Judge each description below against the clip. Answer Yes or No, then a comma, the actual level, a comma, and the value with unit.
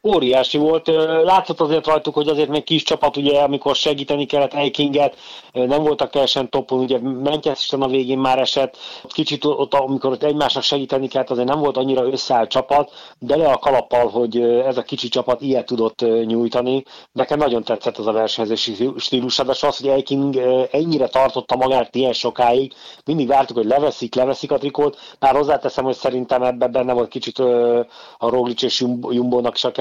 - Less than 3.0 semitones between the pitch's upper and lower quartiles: Yes, narrow, 2.4 semitones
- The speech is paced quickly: Yes, fast, 175 wpm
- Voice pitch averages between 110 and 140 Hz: Yes, low, 135 Hz